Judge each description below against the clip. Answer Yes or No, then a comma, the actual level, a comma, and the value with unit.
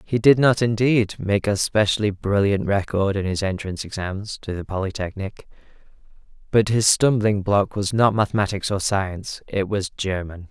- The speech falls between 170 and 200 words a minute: No, average, 155 wpm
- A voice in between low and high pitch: No, low, 100 Hz